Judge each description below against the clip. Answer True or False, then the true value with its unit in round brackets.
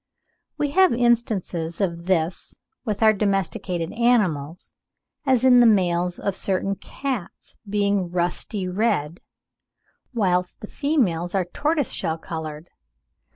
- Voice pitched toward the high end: True (195 Hz)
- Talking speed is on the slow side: True (115 wpm)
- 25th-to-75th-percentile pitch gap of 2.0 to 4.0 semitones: False (5.2 semitones)